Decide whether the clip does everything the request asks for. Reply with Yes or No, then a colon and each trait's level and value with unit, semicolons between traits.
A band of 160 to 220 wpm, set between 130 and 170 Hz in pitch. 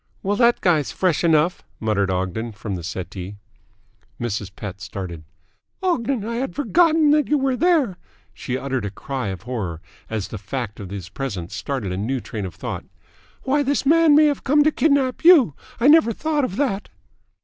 Yes: average, 180 wpm; medium, 140 Hz